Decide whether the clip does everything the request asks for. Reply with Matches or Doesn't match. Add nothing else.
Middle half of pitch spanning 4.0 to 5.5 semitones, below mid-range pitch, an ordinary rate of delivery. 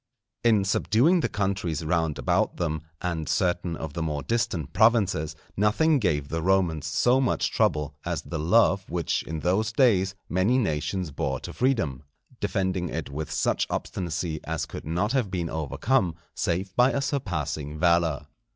Matches